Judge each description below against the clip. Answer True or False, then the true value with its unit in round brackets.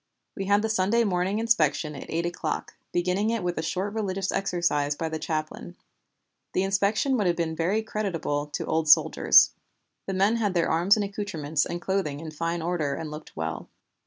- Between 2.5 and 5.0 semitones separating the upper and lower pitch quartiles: True (4.1 semitones)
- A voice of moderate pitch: True (180 Hz)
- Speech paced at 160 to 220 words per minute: True (190 wpm)